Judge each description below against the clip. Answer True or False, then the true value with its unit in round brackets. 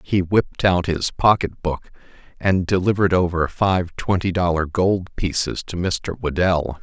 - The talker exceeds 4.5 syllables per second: False (4.3 syllables/s)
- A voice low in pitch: True (90 Hz)